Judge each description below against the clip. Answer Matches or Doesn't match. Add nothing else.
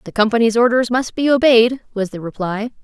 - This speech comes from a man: Doesn't match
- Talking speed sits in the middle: Matches